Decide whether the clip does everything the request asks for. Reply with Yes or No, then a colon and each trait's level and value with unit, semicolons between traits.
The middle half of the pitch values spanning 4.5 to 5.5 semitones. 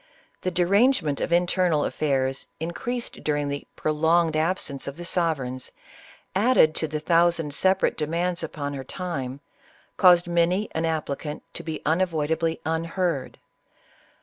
No: average, 2.9 semitones